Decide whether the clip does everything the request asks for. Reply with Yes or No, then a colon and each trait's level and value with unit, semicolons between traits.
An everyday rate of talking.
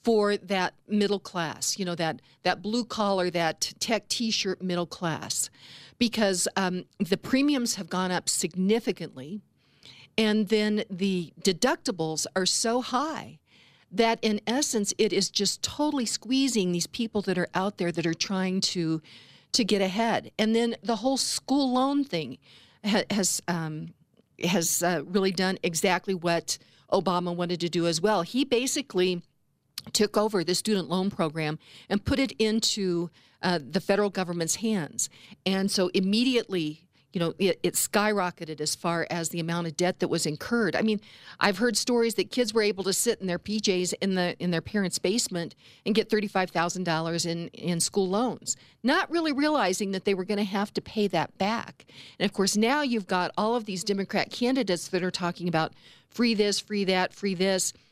Yes: average, 175 wpm